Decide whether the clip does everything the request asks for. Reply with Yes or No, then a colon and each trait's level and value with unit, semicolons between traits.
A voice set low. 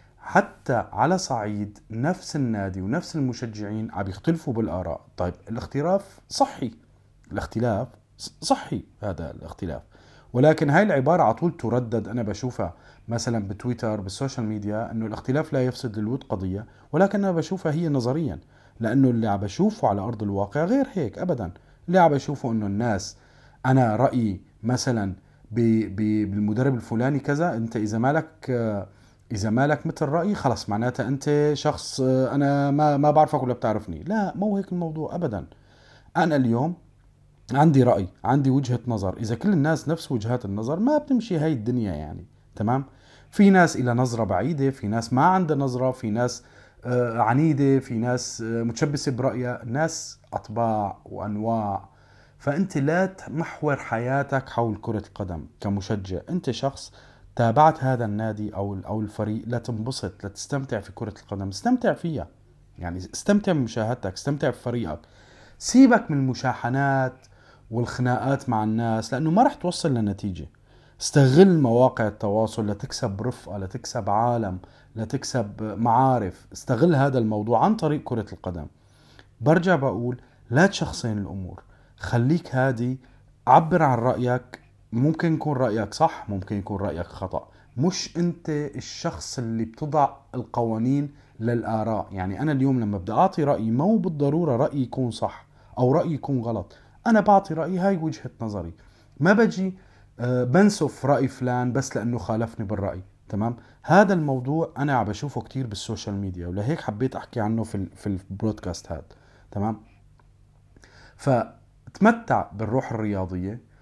Yes: low, 125 Hz